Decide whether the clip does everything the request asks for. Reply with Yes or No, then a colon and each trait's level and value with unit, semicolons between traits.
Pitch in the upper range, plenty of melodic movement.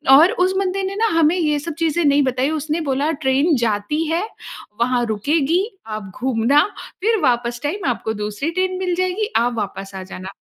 Yes: very high, 290 Hz; wide, 6.4 semitones